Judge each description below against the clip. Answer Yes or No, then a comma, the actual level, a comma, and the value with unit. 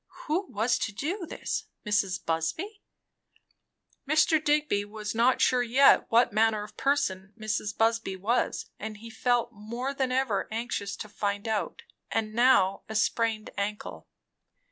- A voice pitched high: Yes, high, 225 Hz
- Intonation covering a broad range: No, average, 3.7 semitones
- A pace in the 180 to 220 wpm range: No, average, 145 wpm